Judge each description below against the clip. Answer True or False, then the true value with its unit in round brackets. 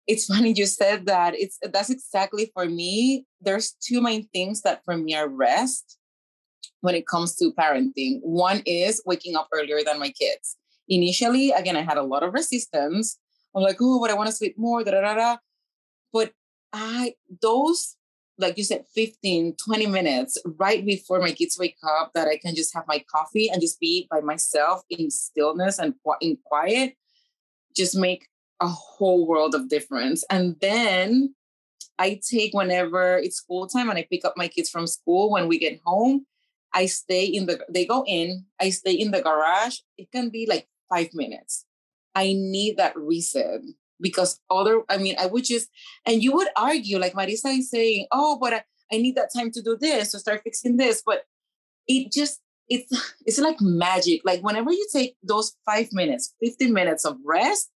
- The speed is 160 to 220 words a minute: True (190 wpm)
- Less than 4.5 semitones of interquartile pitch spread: False (5.4 semitones)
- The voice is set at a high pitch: True (205 Hz)